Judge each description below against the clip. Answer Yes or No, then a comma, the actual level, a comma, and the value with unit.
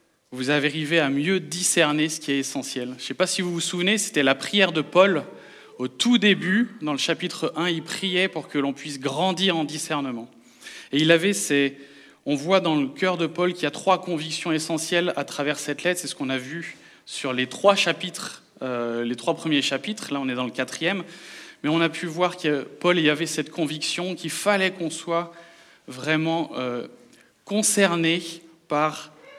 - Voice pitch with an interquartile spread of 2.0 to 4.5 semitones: Yes, average, 3.9 semitones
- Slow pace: No, average, 205 wpm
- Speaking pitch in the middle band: Yes, medium, 160 Hz